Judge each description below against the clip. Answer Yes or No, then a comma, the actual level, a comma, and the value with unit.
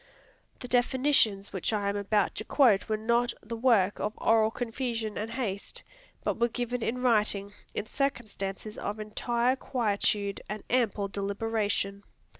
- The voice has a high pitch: Yes, high, 220 Hz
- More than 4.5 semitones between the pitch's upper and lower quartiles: No, average, 3.0 semitones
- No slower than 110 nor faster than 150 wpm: Yes, average, 145 wpm